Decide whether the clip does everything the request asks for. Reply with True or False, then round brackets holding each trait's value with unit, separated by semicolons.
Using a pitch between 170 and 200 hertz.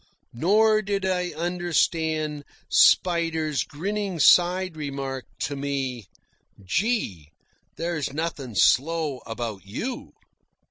False (160 Hz)